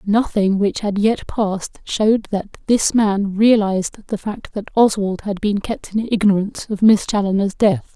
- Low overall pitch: No, high, 205 Hz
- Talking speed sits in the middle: Yes, average, 175 wpm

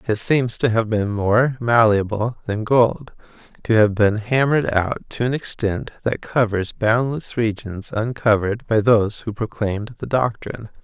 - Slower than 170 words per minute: Yes, average, 155 wpm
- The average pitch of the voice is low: Yes, low, 110 Hz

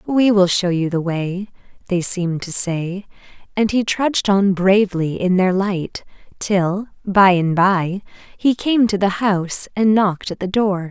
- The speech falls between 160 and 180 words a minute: Yes, average, 175 wpm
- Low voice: No, high, 190 Hz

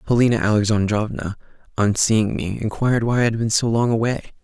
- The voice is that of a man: Yes, male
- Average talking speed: Yes, average, 175 wpm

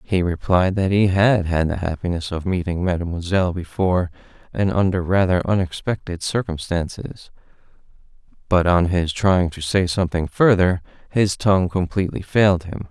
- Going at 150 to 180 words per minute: No, average, 140 wpm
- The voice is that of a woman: No, male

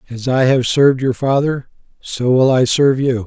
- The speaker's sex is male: Yes, male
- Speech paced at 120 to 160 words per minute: No, average, 200 wpm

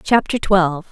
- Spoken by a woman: Yes, female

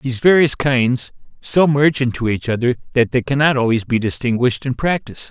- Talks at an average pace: Yes, average, 180 wpm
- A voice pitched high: No, low, 130 Hz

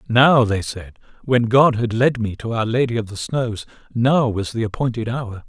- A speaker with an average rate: No, fast, 210 wpm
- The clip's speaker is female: No, male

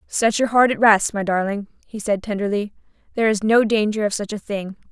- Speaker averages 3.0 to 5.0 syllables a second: No, 5.7 syllables/s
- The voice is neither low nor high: No, high, 210 Hz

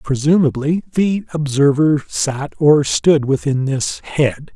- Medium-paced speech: No, slow, 120 wpm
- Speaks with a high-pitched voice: No, medium, 145 Hz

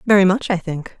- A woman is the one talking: Yes, female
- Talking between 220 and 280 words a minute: Yes, fast, 240 wpm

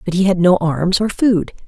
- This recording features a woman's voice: Yes, female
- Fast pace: Yes, fast, 250 wpm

